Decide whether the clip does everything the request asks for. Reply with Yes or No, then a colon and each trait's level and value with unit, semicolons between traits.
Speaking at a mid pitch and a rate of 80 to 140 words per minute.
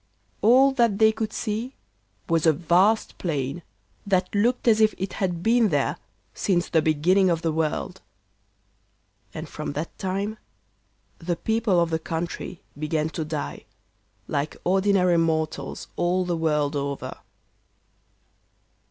Yes: medium, 175 Hz; slow, 135 wpm